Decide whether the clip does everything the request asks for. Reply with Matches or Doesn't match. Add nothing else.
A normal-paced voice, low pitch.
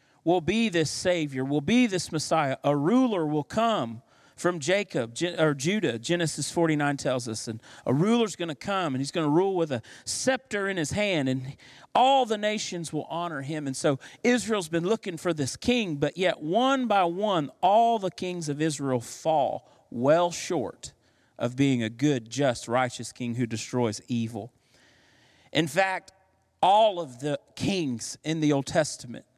Doesn't match